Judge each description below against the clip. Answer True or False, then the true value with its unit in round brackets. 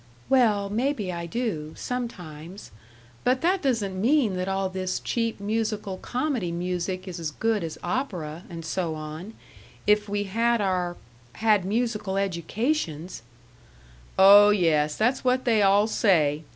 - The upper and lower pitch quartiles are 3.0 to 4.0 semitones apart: False (4.8 semitones)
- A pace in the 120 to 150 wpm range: True (140 wpm)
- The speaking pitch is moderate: False (195 Hz)